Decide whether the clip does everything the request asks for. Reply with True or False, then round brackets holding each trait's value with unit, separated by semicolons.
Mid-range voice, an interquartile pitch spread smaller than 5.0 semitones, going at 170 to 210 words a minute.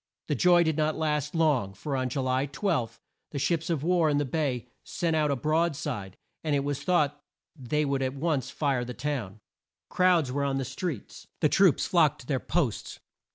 True (145 Hz; 3.5 semitones; 200 wpm)